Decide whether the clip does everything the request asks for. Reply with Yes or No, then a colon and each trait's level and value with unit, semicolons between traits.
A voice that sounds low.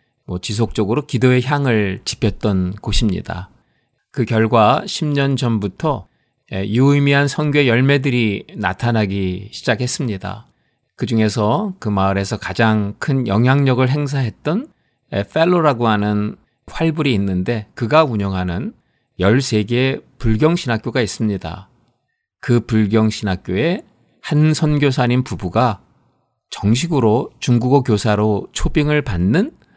Yes: low, 115 Hz